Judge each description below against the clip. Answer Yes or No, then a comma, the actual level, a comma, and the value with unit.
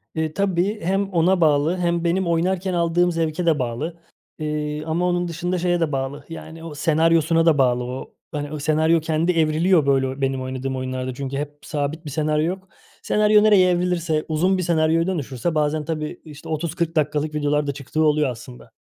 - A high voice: No, medium, 160 Hz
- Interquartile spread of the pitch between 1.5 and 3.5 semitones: Yes, average, 2.8 semitones